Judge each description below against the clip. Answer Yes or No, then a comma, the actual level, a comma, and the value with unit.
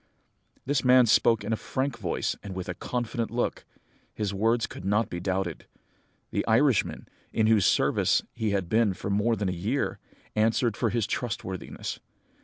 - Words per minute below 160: No, average, 170 wpm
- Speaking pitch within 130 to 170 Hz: No, low, 110 Hz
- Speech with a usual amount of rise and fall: Yes, average, 3.3 semitones